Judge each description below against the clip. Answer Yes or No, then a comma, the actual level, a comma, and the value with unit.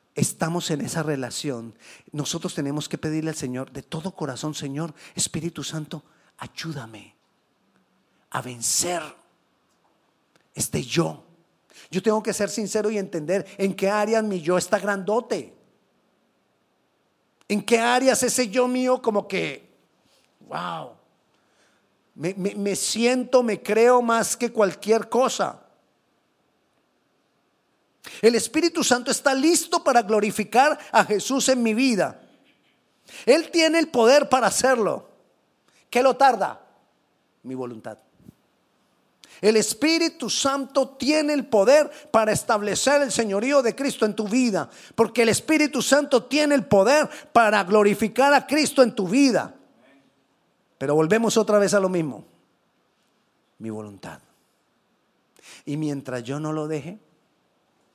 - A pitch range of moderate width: No, wide, 7.3 semitones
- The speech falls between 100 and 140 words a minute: Yes, slow, 125 wpm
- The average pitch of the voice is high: Yes, high, 215 Hz